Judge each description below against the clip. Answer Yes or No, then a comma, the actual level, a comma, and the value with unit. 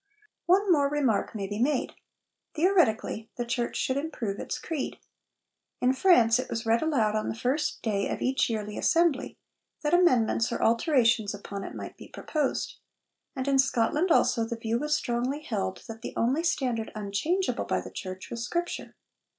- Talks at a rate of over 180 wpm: No, average, 170 wpm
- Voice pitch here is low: No, high, 245 Hz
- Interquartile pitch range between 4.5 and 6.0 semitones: Yes, average, 5.1 semitones